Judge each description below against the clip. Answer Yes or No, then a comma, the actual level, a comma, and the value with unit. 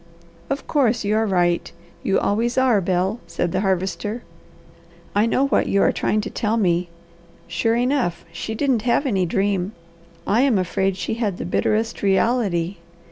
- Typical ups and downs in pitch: Yes, average, 4.0 semitones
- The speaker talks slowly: No, average, 165 wpm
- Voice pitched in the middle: No, high, 205 Hz